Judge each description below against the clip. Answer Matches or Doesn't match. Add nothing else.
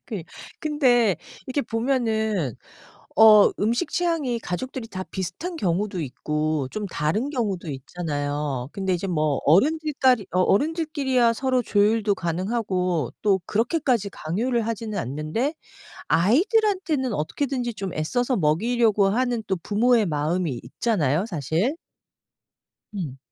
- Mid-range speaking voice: Doesn't match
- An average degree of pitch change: Doesn't match